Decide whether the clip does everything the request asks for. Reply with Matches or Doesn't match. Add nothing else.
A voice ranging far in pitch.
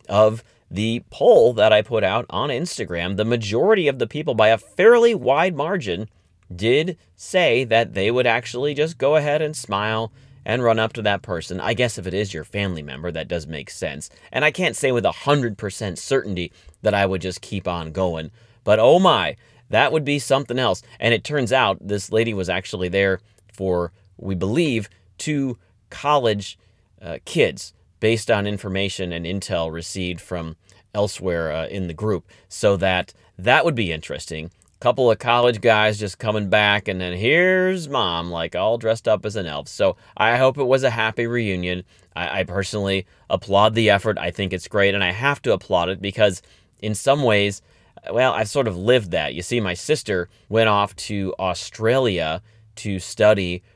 Doesn't match